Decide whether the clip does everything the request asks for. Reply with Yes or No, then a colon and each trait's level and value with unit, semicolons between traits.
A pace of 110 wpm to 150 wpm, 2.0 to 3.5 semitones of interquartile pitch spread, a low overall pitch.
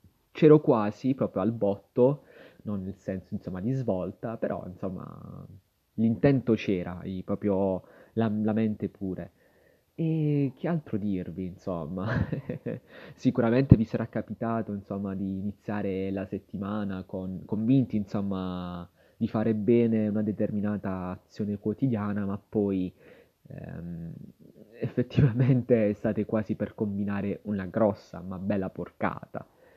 Yes: slow, 115 wpm; average, 2.9 semitones; low, 105 Hz